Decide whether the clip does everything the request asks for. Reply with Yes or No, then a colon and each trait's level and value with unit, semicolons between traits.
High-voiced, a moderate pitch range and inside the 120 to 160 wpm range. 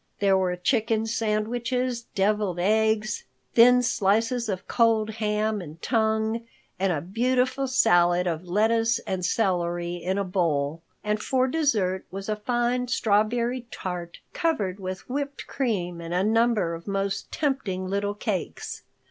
Yes: high, 210 Hz; average, 4.0 semitones; average, 140 wpm